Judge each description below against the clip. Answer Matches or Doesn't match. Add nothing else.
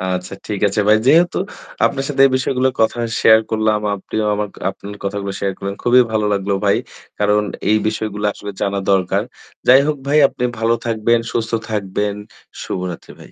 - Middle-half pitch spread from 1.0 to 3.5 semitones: Matches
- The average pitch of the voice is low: Matches